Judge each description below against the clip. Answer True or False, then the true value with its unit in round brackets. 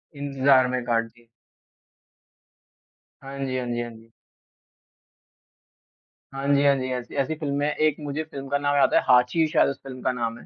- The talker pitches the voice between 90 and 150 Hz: True (135 Hz)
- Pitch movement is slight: True (2.3 semitones)